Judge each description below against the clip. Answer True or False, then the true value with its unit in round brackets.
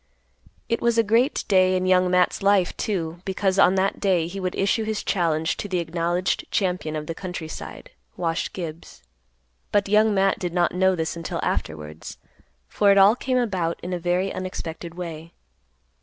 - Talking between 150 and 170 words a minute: False (180 wpm)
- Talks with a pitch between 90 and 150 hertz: False (185 Hz)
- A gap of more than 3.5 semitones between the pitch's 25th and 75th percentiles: False (2.7 semitones)